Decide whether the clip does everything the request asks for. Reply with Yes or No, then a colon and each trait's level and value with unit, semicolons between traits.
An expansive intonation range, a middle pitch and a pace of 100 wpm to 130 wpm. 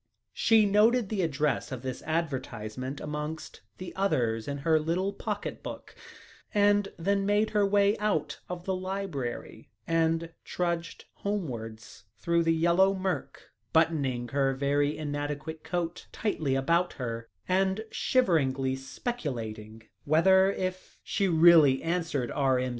Yes: wide, 5.9 semitones; medium, 165 Hz; slow, 125 wpm